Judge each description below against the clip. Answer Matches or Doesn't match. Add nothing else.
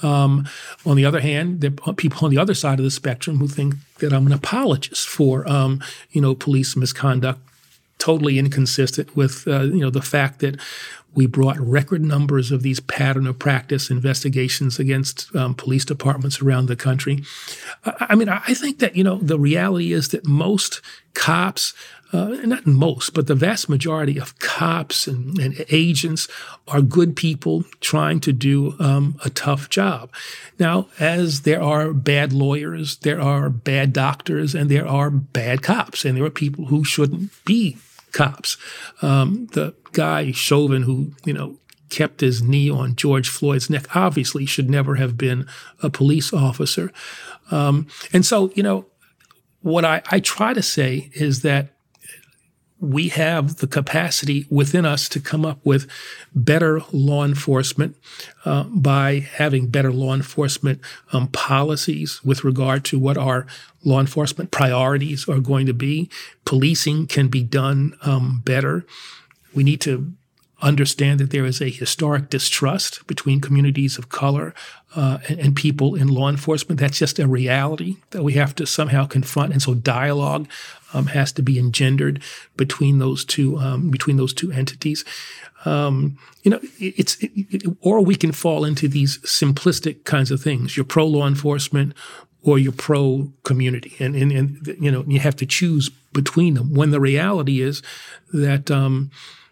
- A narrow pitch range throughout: Matches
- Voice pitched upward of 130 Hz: Matches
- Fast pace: Doesn't match